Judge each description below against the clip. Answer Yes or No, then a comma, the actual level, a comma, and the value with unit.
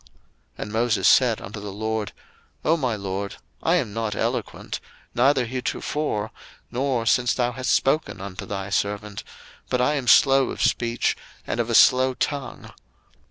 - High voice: No, low, 115 Hz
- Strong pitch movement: No, average, 3.8 semitones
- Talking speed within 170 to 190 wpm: No, average, 160 wpm